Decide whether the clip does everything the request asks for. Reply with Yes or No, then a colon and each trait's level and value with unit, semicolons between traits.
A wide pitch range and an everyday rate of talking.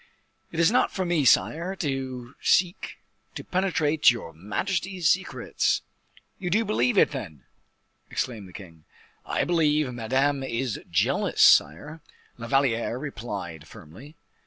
No: wide, 7.0 semitones; slow, 130 wpm